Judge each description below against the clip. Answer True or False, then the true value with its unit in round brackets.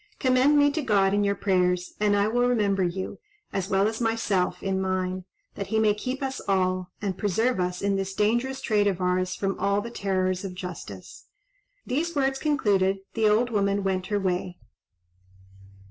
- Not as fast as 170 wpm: False (180 wpm)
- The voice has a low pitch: False (200 Hz)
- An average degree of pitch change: True (3.2 semitones)